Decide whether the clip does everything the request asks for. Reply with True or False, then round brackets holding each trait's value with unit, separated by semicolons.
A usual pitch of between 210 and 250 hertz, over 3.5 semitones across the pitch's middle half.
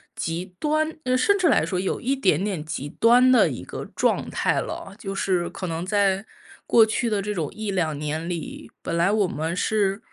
False (195 Hz; 4.5 semitones)